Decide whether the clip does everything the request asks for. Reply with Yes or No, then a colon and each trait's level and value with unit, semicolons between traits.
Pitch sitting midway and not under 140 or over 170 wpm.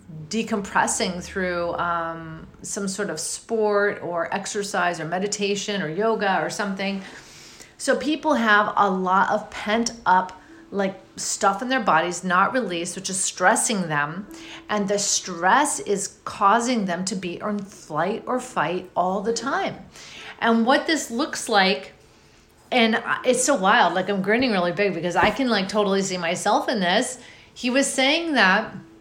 No: high, 205 Hz; average, 155 wpm